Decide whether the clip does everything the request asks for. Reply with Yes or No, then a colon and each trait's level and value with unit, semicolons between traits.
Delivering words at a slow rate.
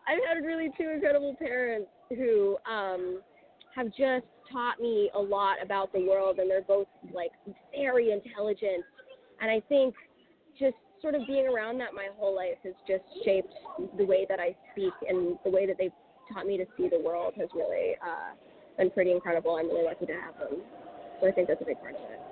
No: average, 200 wpm